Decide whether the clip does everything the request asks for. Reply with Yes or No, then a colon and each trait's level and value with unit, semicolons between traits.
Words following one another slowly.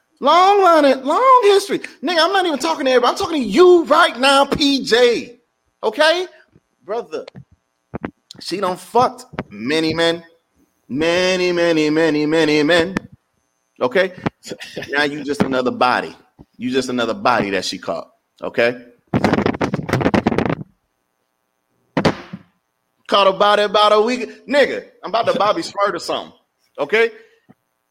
Yes: slow, 130 wpm